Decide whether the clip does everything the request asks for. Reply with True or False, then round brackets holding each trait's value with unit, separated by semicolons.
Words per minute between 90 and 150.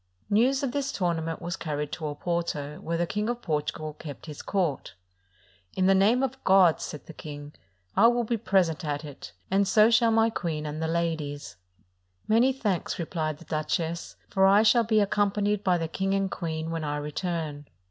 False (190 wpm)